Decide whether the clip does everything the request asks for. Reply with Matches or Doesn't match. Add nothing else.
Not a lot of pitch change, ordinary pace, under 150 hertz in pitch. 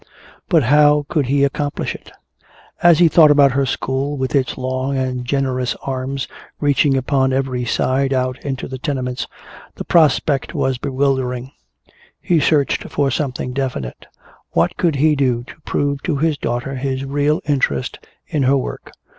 Matches